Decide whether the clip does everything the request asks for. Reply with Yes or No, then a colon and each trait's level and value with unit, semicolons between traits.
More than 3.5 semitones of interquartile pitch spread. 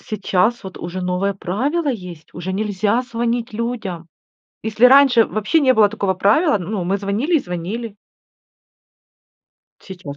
Yes: average, 4.4 semitones